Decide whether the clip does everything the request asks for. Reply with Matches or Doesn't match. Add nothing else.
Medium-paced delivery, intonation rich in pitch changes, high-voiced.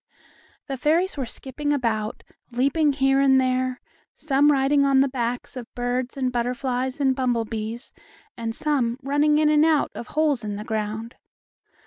Doesn't match